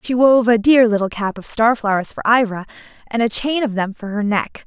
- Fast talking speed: Yes, fast, 245 wpm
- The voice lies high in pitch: Yes, high, 225 Hz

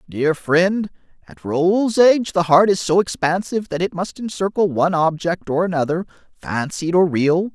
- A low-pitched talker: No, medium, 175 Hz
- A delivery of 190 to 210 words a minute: No, average, 165 wpm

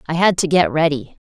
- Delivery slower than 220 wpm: No, fast, 235 wpm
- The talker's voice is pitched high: No, medium, 160 Hz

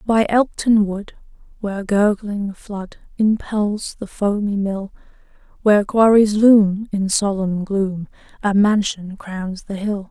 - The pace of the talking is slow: Yes, slow, 125 wpm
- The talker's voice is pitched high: Yes, high, 205 Hz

